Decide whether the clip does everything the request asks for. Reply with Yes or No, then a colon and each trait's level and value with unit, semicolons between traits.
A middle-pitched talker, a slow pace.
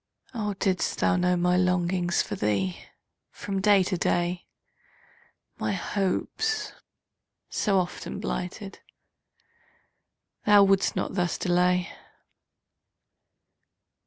Yes: medium, 180 Hz; slow, 95 wpm